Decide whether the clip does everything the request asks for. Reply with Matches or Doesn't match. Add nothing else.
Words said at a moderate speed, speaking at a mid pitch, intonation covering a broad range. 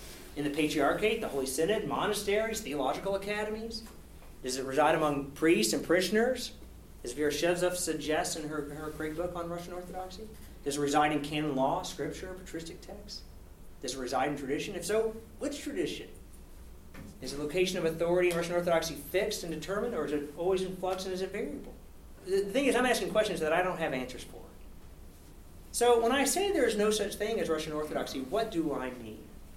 Matches